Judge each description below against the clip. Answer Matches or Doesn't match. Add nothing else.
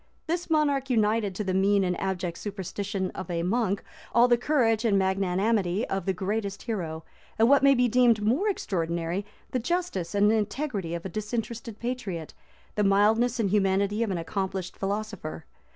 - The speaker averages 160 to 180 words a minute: Matches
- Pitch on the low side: Doesn't match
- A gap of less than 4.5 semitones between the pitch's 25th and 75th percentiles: Matches